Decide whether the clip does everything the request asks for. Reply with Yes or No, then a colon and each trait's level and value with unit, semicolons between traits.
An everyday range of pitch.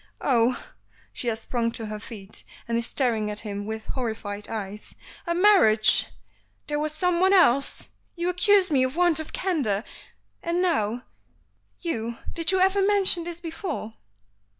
No: wide, 8.1 semitones